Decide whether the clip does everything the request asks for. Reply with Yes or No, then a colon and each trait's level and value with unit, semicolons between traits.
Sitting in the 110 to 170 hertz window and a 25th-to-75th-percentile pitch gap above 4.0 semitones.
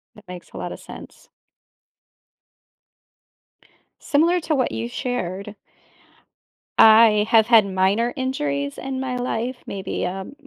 No: high, 220 Hz; average, 5.2 semitones